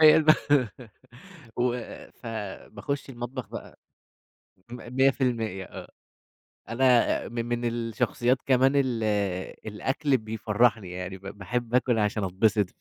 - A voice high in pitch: No, low, 120 Hz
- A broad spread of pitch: No, average, 2.8 semitones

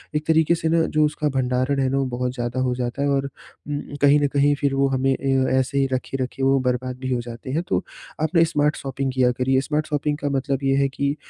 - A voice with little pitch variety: Yes, narrow, 2.0 semitones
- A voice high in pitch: No, low, 135 Hz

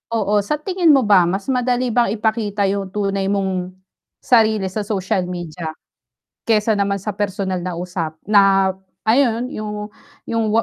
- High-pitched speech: Yes, high, 205 Hz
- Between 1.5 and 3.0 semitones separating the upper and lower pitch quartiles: Yes, narrow, 2.6 semitones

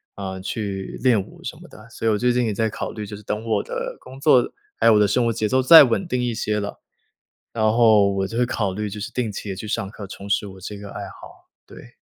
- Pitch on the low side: Yes, low, 105 Hz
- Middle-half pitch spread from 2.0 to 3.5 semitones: Yes, average, 2.8 semitones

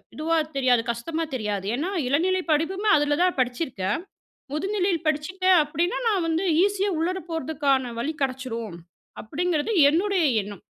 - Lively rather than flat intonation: Yes, wide, 5.9 semitones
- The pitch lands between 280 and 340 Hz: Yes, very high, 310 Hz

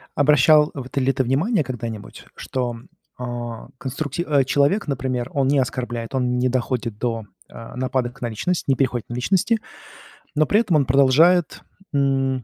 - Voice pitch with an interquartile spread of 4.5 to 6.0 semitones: No, average, 2.8 semitones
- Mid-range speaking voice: No, low, 130 Hz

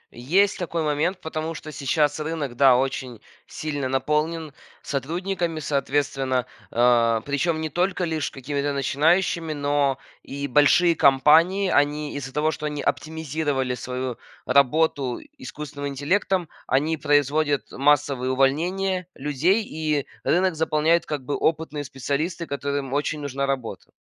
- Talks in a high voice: No, medium, 145 Hz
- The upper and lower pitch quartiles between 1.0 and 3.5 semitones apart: Yes, average, 2.8 semitones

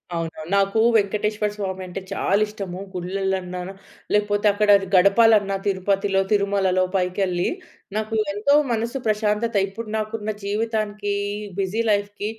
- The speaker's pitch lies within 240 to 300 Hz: No, high, 205 Hz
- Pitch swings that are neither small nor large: No, narrow, 1.8 semitones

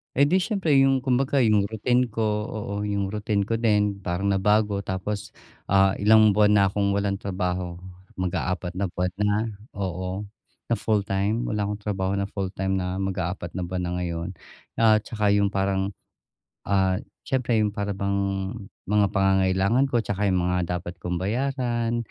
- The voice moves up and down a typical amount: No, narrow, 2.2 semitones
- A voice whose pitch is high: No, low, 100 Hz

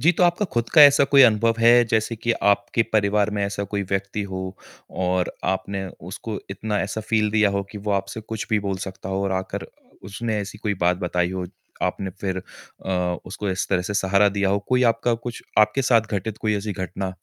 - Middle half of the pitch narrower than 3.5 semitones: Yes, narrow, 2.5 semitones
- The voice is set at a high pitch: No, low, 100 Hz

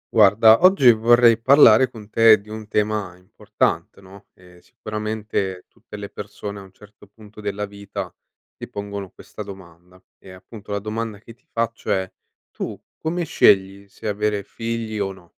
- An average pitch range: No, narrow, 2.1 semitones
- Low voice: Yes, low, 105 Hz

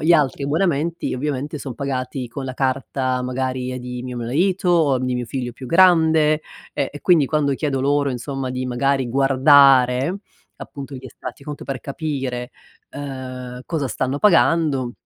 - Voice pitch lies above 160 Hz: No, low, 135 Hz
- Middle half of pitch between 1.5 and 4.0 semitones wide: Yes, narrow, 2.6 semitones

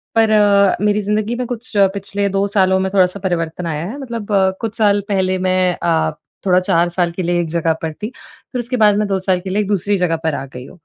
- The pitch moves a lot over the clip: No, average, 3.0 semitones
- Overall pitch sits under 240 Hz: Yes, high, 190 Hz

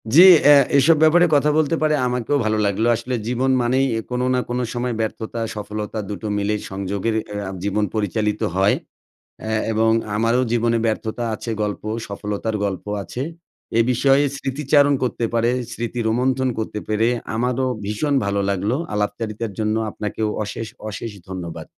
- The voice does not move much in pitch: No, average, 3.2 semitones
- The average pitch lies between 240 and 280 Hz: No, low, 115 Hz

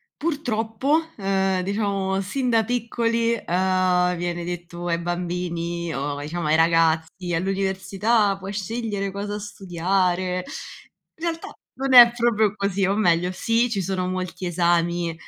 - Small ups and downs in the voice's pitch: No, average, 3.7 semitones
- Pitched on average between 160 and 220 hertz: Yes, high, 190 Hz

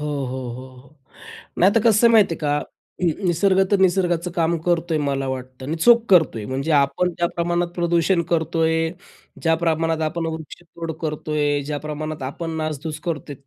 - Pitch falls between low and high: Yes, medium, 160 Hz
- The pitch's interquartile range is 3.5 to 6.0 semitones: No, average, 2.8 semitones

